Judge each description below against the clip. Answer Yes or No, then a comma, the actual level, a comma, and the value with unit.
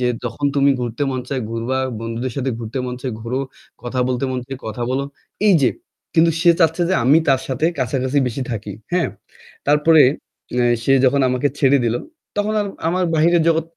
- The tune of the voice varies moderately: Yes, average, 3.8 semitones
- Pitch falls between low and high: No, low, 130 Hz